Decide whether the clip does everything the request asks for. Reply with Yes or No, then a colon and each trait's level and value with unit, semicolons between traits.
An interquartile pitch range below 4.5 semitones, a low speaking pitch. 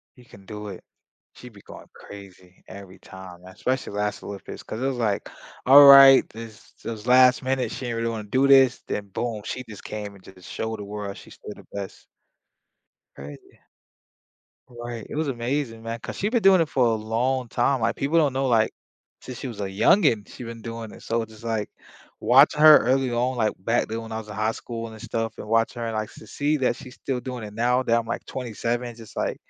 Yes: average, 3.2 semitones; low, 115 Hz